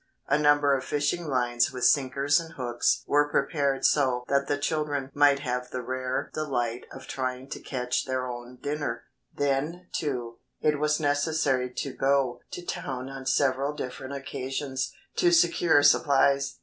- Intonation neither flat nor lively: No, narrow, 2.3 semitones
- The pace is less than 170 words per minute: Yes, average, 155 wpm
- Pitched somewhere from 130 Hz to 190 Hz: Yes, medium, 140 Hz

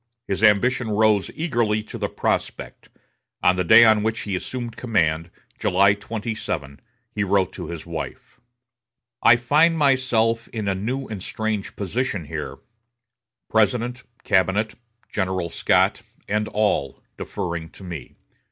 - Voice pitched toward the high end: No, low, 105 Hz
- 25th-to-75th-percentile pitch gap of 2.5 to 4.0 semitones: Yes, average, 3.6 semitones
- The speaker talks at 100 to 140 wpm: Yes, slow, 135 wpm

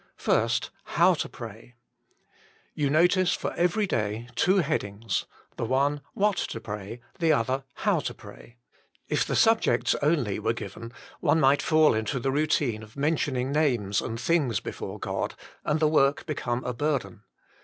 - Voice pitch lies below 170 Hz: Yes, low, 135 Hz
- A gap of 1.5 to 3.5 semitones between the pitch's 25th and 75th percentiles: No, average, 5.3 semitones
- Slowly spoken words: No, average, 155 wpm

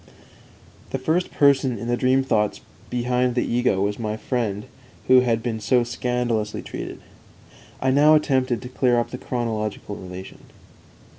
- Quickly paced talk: No, average, 150 wpm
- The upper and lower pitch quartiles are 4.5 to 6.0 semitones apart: No, average, 2.7 semitones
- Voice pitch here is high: No, low, 120 Hz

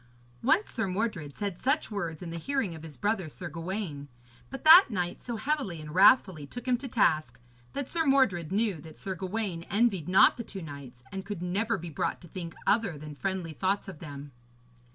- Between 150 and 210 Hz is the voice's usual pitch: Yes, high, 190 Hz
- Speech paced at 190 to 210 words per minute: Yes, average, 200 wpm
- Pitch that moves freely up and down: Yes, wide, 5.7 semitones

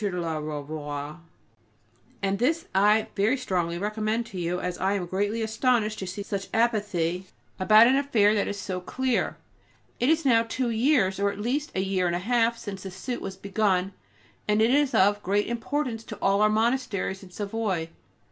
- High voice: Yes, high, 205 Hz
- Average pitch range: Yes, average, 3.5 semitones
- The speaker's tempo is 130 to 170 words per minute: No, average, 185 wpm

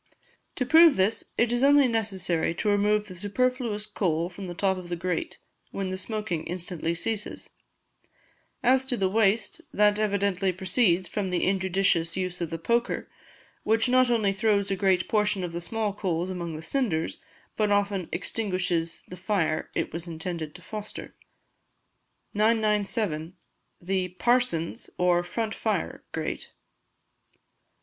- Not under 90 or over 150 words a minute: Yes, average, 145 wpm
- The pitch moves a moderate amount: Yes, average, 3.5 semitones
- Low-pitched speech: No, high, 195 Hz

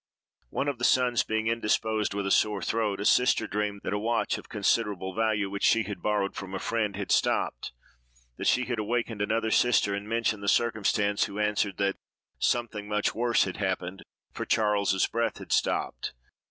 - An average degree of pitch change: No, narrow, 2.2 semitones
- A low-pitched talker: Yes, low, 105 Hz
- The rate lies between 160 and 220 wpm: Yes, average, 185 wpm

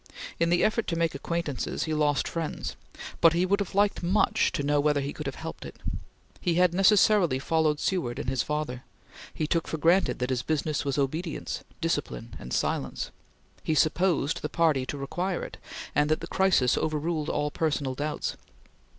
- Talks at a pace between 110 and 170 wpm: No, average, 185 wpm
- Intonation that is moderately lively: Yes, average, 3.1 semitones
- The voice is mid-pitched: Yes, medium, 155 Hz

